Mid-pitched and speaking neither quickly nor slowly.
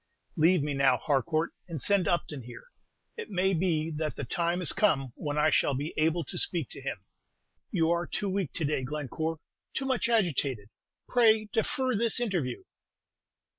Yes: medium, 165 Hz; average, 170 wpm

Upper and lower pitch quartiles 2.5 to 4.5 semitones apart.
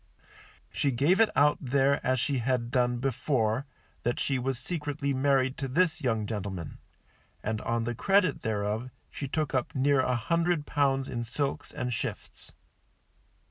Yes: average, 3.2 semitones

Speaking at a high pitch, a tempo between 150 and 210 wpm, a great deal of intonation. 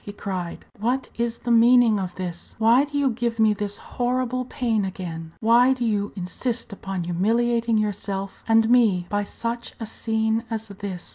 No: high, 220 Hz; average, 170 wpm; average, 3.1 semitones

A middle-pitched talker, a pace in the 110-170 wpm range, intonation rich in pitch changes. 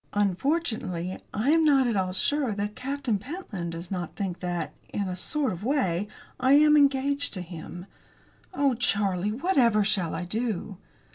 No: high, 210 Hz; average, 160 wpm; wide, 7.2 semitones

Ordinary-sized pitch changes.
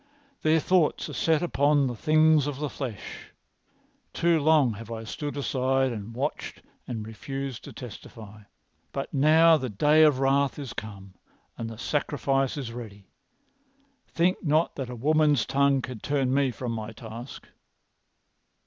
Yes: average, 4.4 semitones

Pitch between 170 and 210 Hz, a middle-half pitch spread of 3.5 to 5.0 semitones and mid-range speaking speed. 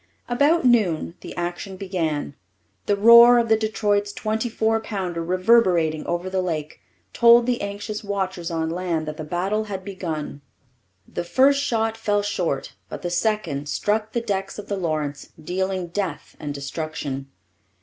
Yes: high, 190 Hz; average, 4.7 semitones; average, 155 wpm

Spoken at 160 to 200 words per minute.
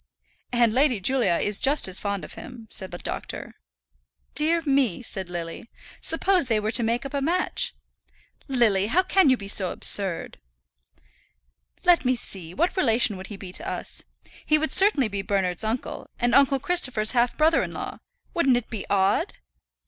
Yes: average, 175 wpm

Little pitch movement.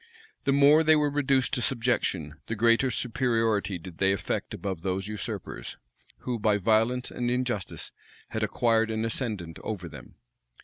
No: average, 4.5 semitones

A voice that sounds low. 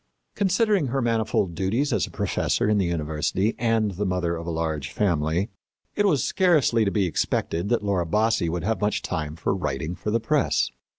Yes: low, 100 Hz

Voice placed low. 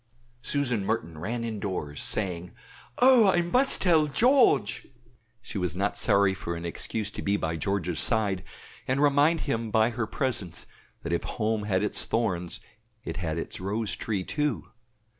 Yes: low, 105 Hz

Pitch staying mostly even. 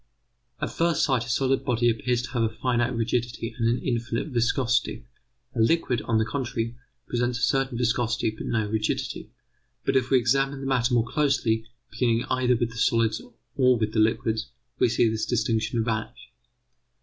Yes: narrow, 1.9 semitones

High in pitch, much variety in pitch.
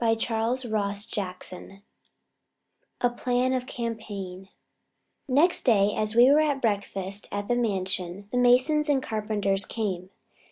No: high, 220 Hz; average, 3.9 semitones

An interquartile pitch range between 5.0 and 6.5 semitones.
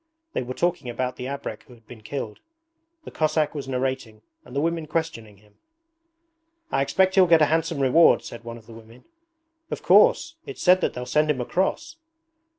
Yes: wide, 5.5 semitones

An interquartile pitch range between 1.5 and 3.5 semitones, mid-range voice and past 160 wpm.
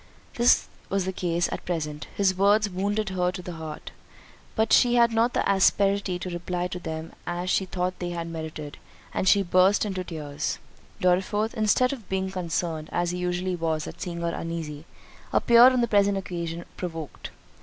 Yes: average, 3.0 semitones; medium, 180 Hz; average, 175 wpm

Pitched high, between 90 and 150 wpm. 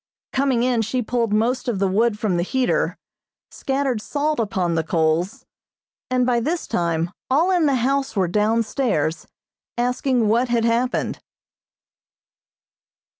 Yes: high, 235 Hz; average, 140 wpm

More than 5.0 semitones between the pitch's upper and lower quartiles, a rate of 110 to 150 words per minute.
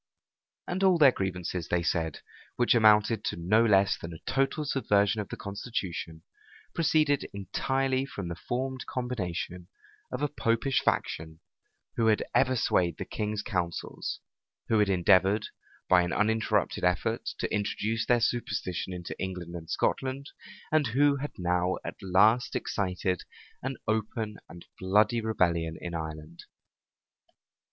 Yes: wide, 5.5 semitones; average, 140 wpm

